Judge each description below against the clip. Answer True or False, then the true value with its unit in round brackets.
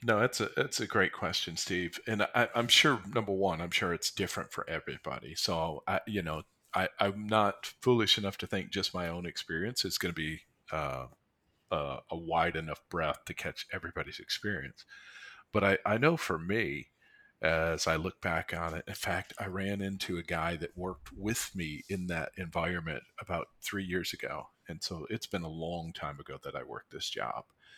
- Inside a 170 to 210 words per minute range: True (200 wpm)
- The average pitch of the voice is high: False (90 Hz)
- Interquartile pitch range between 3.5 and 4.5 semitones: True (3.9 semitones)